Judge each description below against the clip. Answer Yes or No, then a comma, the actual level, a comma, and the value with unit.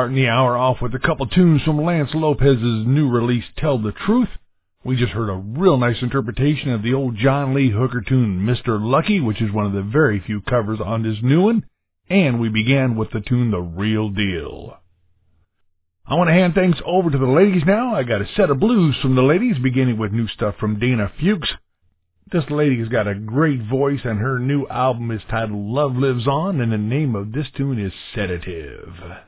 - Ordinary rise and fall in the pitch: Yes, average, 4.8 semitones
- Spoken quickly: Yes, fast, 210 wpm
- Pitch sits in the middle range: No, low, 125 Hz